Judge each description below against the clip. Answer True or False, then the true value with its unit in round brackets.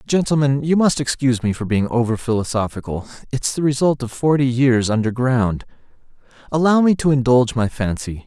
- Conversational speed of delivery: True (160 wpm)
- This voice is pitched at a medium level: False (130 Hz)